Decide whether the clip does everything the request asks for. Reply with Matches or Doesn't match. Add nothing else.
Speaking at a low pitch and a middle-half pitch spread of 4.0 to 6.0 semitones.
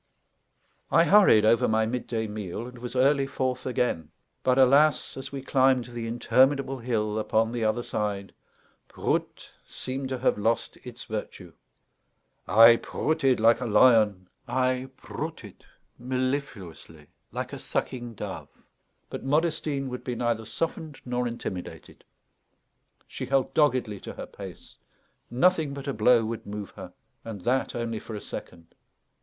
Doesn't match